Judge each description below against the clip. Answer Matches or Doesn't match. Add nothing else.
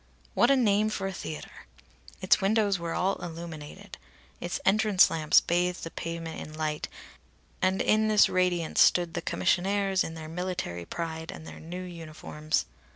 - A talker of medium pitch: Matches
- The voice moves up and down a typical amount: Matches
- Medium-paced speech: Matches